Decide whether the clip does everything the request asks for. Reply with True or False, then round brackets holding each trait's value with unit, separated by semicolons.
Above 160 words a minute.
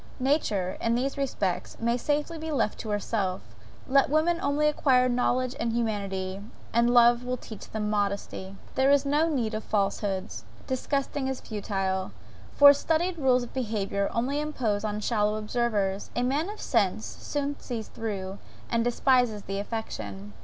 False (155 wpm)